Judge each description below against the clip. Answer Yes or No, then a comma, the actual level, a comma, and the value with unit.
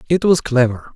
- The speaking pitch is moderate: Yes, medium, 145 Hz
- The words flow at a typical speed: Yes, average, 190 wpm